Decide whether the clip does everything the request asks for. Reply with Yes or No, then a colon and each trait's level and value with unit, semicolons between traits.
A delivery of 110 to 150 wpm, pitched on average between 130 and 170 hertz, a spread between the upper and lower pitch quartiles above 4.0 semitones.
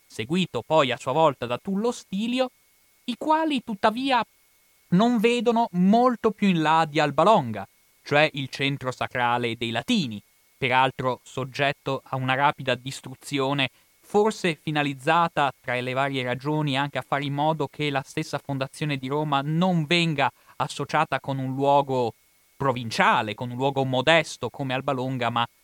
Yes: average, 145 wpm; medium, 140 Hz; average, 4.5 semitones